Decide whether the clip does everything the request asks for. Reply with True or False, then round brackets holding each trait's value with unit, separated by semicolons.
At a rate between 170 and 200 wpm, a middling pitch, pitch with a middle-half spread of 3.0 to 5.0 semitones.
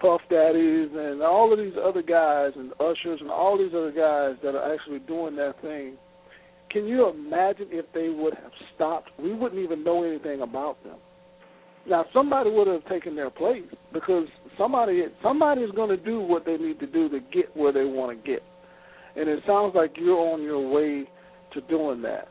True (195 wpm; 170 Hz; 3.6 semitones)